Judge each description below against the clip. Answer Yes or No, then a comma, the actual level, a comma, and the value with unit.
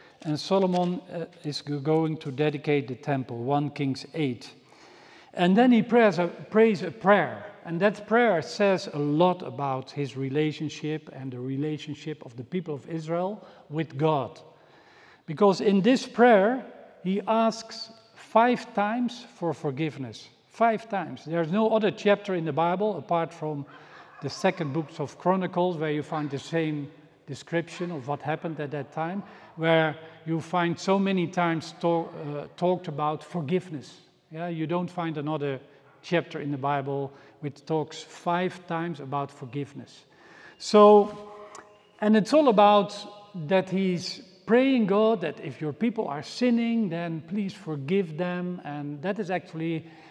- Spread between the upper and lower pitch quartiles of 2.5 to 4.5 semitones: No, average, 5.1 semitones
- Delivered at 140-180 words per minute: Yes, average, 150 wpm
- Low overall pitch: No, medium, 170 Hz